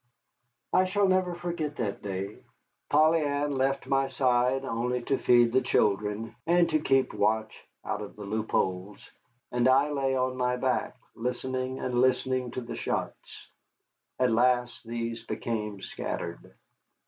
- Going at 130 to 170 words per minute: Yes, average, 145 wpm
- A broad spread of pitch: No, average, 3.2 semitones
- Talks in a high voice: No, low, 125 Hz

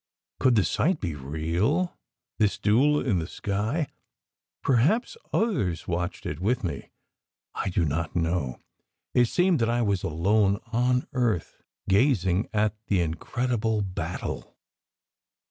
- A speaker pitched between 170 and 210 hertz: No, low, 105 Hz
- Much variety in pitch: Yes, wide, 6.2 semitones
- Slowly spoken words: Yes, slow, 130 wpm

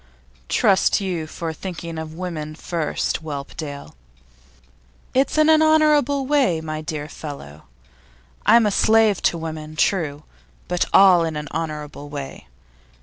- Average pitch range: Yes, average, 4.6 semitones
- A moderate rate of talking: No, slow, 130 wpm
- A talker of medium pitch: Yes, medium, 165 Hz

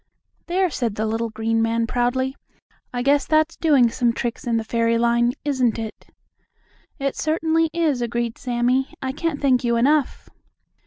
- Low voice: No, high, 245 Hz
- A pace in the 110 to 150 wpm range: No, average, 160 wpm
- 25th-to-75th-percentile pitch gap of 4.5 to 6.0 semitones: No, average, 3.7 semitones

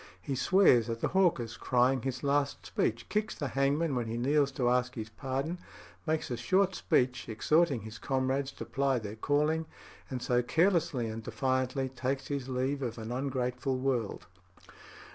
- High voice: No, low, 130 Hz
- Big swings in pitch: No, average, 2.7 semitones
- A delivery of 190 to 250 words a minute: No, average, 165 wpm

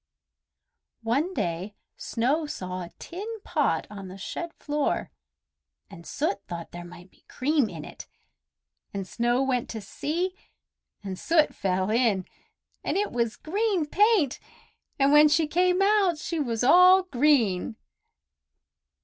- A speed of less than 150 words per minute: Yes, slow, 135 wpm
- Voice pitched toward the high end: Yes, very high, 270 Hz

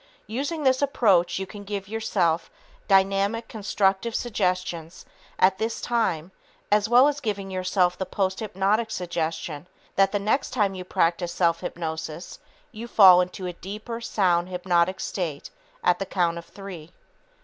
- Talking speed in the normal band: Yes, average, 150 wpm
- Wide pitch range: No, average, 3.4 semitones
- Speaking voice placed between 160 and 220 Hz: Yes, high, 190 Hz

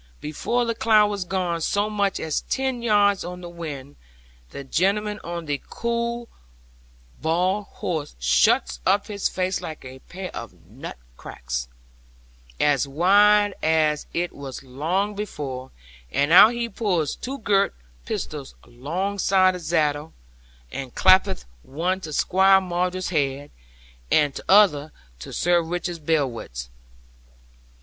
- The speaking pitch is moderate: Yes, medium, 175 Hz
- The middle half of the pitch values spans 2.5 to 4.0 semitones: No, wide, 5.4 semitones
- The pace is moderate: No, slow, 130 wpm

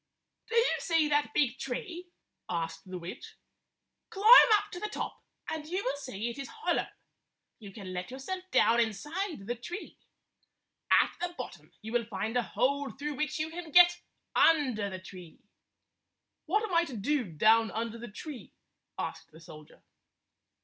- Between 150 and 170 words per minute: Yes, average, 165 wpm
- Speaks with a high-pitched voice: Yes, very high, 265 Hz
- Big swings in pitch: Yes, wide, 7.7 semitones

